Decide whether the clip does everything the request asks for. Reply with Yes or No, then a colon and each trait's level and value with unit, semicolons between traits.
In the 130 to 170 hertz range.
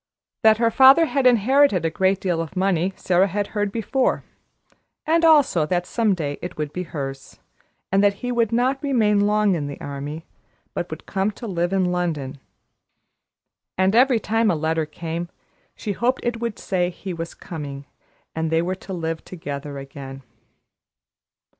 No: medium, 185 Hz